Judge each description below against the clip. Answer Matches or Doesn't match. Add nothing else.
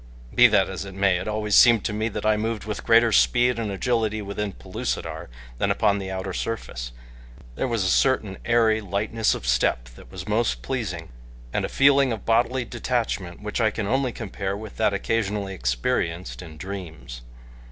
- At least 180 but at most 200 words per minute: Matches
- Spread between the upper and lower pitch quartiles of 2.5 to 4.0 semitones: Matches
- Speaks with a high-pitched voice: Doesn't match